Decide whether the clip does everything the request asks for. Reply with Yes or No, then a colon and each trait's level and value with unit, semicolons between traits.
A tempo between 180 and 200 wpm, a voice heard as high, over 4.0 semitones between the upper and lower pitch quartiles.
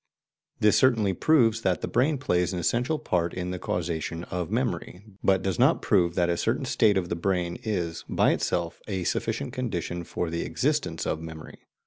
No: average, 185 wpm; very low, 90 Hz; average, 4.6 semitones